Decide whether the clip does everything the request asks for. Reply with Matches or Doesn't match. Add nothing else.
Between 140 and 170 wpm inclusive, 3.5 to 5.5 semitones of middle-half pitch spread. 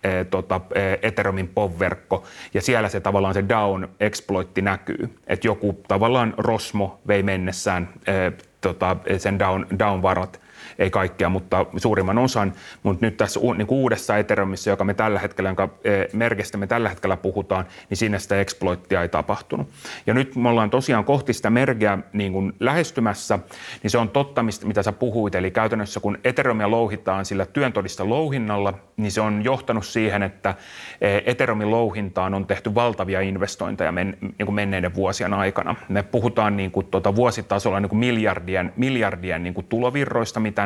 Doesn't match